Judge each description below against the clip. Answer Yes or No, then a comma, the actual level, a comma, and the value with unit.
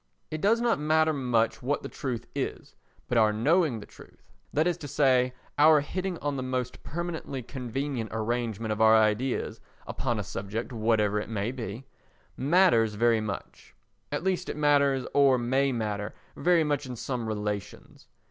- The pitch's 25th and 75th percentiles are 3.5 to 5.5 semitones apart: Yes, average, 4.8 semitones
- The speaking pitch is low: Yes, low, 130 Hz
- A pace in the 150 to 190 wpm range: Yes, average, 160 wpm